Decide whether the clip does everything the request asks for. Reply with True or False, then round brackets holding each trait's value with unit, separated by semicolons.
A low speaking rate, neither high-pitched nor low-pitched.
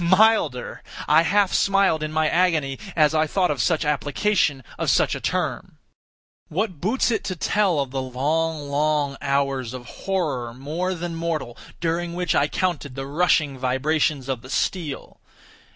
False (160 wpm; 155 Hz)